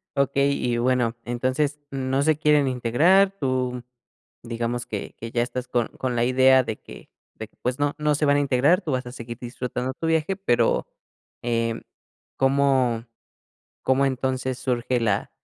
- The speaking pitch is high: No, low, 130 Hz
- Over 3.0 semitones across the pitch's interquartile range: No, narrow, 2.6 semitones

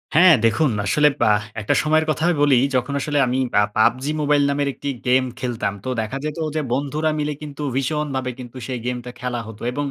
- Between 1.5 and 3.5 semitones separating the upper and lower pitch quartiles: Yes, average, 3.2 semitones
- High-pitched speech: No, low, 135 Hz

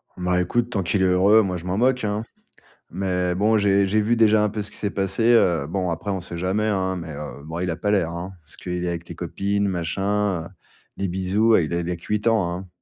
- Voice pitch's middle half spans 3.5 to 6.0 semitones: No, average, 3.0 semitones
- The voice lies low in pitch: Yes, very low, 95 Hz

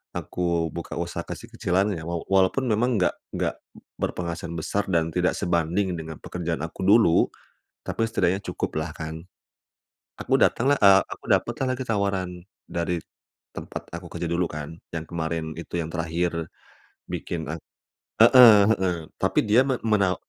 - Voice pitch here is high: No, very low, 90 Hz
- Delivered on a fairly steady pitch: No, average, 3.4 semitones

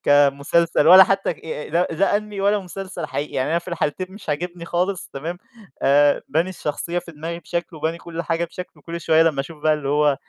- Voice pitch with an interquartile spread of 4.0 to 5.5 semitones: No, average, 3.0 semitones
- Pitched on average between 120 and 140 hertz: No, medium, 170 Hz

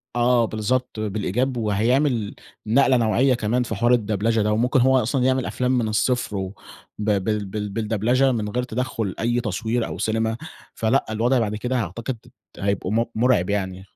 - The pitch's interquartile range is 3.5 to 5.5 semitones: No, average, 2.8 semitones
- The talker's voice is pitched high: No, low, 115 Hz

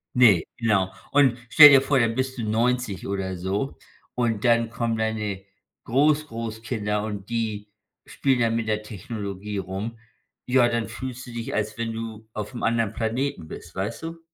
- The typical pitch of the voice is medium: No, low, 115 Hz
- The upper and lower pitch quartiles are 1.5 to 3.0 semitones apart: Yes, average, 2.7 semitones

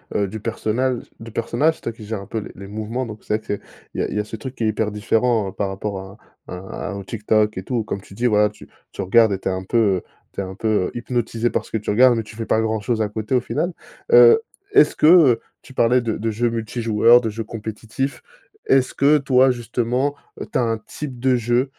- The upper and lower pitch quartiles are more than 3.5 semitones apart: No, average, 2.7 semitones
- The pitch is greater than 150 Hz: No, low, 115 Hz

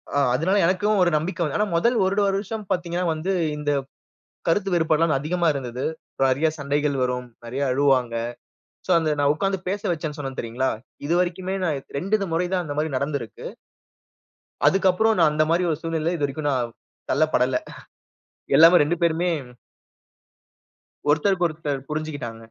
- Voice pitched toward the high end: No, medium, 155 Hz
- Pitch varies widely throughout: No, average, 4.1 semitones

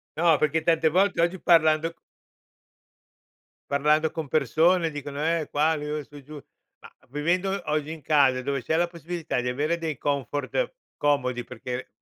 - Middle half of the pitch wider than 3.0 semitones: No, average, 2.7 semitones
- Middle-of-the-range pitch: Yes, medium, 155 Hz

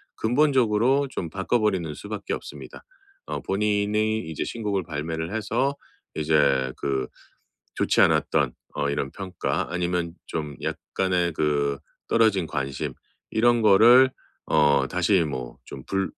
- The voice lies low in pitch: Yes, very low, 95 Hz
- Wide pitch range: Yes, wide, 6.0 semitones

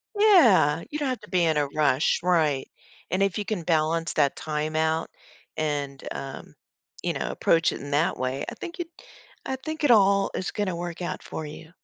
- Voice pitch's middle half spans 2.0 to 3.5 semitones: No, average, 4.8 semitones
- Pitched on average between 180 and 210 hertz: No, medium, 165 Hz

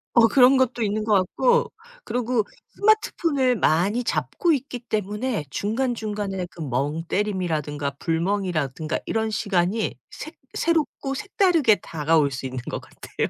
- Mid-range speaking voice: No, high, 210 Hz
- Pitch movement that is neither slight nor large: No, wide, 7.6 semitones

